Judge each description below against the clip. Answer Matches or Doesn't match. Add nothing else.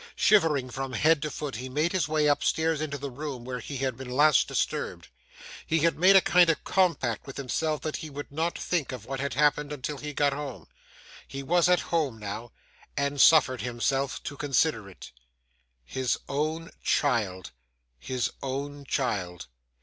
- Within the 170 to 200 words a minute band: Matches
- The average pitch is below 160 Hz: Matches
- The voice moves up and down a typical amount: Matches